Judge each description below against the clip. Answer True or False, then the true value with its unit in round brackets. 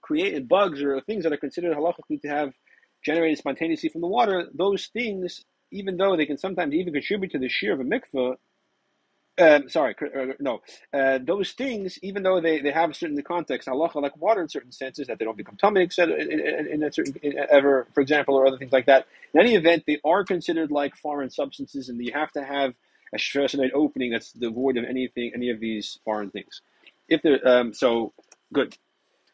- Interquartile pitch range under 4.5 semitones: False (4.9 semitones)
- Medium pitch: True (145 Hz)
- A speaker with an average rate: False (210 wpm)